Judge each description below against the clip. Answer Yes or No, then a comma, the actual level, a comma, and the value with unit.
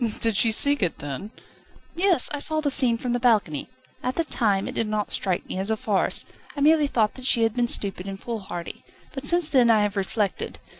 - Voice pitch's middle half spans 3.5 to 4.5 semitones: No, average, 5.2 semitones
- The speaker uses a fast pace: Yes, fast, 220 wpm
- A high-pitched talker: Yes, high, 225 Hz